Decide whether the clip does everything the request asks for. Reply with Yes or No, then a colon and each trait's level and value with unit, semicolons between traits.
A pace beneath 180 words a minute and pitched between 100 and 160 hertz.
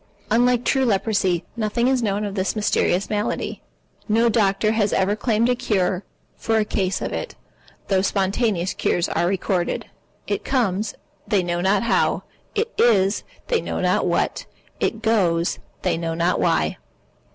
No: average, 155 wpm; high, 205 Hz